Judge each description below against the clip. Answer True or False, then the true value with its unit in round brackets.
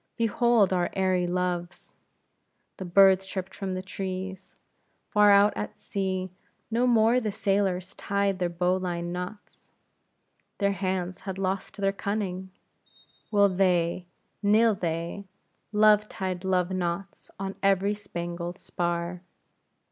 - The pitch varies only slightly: True (1.9 semitones)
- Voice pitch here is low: False (190 Hz)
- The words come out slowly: True (120 wpm)